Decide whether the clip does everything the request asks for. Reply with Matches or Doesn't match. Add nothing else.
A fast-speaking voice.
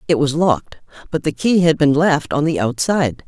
Matches